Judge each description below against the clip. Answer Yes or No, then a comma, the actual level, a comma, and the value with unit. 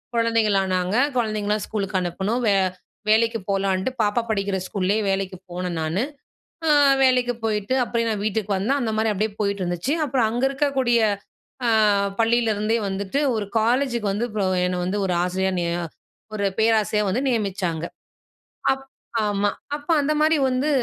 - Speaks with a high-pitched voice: Yes, high, 210 Hz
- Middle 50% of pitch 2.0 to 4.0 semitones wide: Yes, average, 3.4 semitones